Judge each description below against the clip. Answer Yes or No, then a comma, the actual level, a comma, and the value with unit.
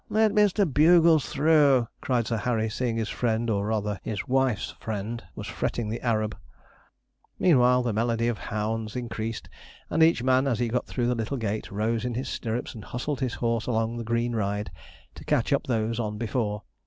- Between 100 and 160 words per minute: No, average, 190 wpm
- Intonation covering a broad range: No, narrow, 2.5 semitones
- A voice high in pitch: No, low, 115 Hz